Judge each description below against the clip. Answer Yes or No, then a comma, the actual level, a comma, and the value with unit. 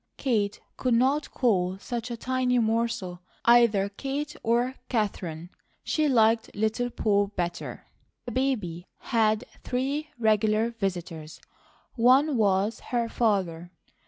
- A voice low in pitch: No, high, 225 Hz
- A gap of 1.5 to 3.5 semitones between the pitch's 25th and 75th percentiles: No, average, 3.9 semitones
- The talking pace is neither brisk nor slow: No, slow, 115 wpm